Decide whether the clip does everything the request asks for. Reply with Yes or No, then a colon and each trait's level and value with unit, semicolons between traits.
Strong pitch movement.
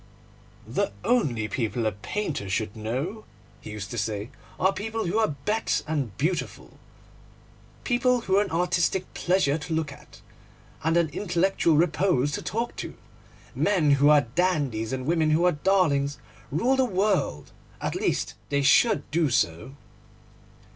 Yes: wide, 6.7 semitones